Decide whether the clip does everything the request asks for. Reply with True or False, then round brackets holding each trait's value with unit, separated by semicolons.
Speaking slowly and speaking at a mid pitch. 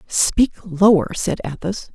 True (125 wpm; 180 Hz)